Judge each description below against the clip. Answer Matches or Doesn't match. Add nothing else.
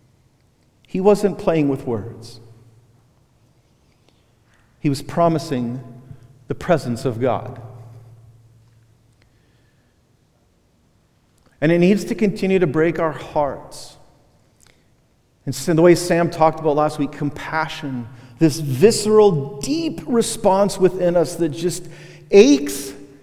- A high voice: Doesn't match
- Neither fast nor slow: Doesn't match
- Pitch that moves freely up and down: Matches